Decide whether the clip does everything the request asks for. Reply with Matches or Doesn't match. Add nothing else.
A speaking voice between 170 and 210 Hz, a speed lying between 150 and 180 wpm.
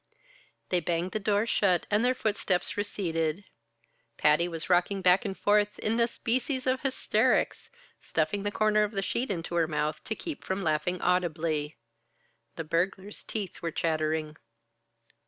Matches